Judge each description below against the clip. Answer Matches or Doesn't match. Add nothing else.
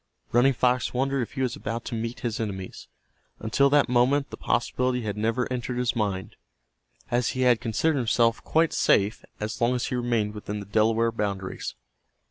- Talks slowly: Doesn't match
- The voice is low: Matches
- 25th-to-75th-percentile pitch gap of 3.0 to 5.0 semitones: Doesn't match